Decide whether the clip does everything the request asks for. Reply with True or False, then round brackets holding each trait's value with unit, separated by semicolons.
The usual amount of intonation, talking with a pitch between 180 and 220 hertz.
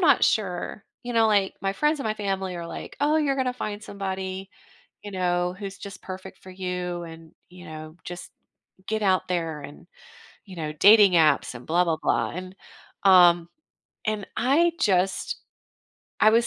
True (3.3 semitones; 190 Hz)